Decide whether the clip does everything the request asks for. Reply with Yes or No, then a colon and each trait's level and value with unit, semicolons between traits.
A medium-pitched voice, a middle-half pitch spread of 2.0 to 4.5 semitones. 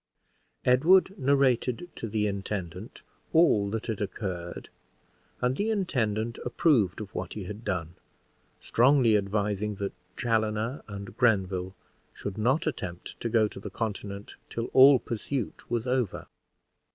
No: low, 110 Hz; average, 3.9 semitones